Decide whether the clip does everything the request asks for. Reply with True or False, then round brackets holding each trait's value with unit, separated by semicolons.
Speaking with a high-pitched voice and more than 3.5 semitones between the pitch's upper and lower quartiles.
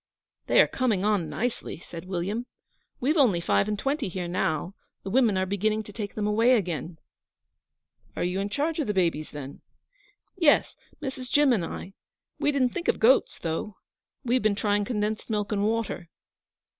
True (210 Hz; 4.9 semitones)